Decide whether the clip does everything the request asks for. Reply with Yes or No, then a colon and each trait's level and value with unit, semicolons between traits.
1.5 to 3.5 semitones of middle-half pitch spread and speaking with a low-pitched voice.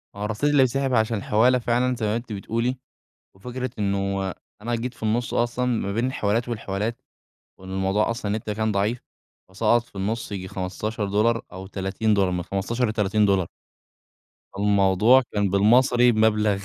Yes: average, 3.2 semitones; low, 110 Hz